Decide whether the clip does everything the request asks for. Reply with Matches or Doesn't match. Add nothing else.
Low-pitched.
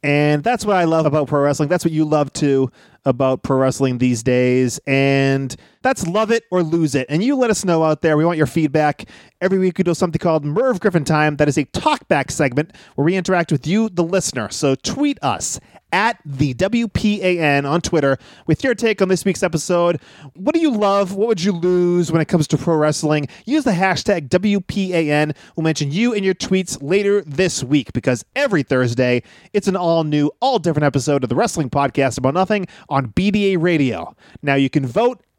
Doesn't match